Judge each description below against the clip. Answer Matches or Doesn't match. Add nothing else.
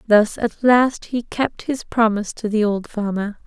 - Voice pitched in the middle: Doesn't match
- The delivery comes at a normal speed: Matches